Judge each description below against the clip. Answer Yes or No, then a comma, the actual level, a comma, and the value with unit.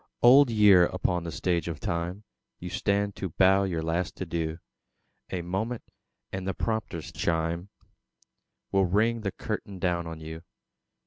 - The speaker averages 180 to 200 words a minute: No, average, 145 wpm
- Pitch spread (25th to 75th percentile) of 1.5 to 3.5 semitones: Yes, average, 3.0 semitones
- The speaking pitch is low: Yes, very low, 90 Hz